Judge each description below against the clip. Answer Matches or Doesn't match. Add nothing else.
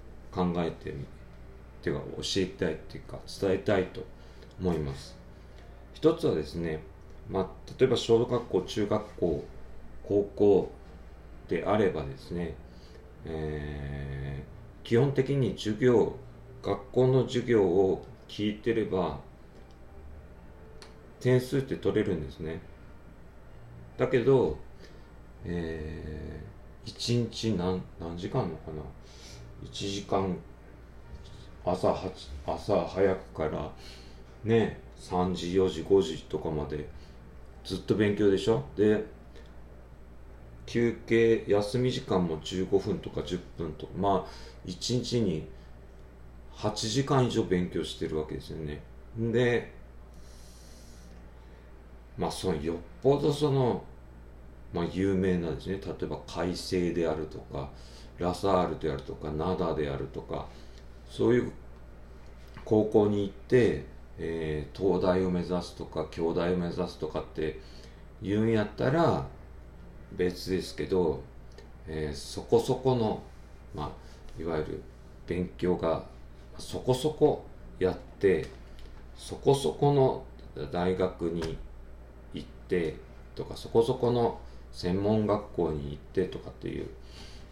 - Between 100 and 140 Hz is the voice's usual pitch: Doesn't match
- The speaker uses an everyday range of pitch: Doesn't match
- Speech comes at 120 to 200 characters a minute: Matches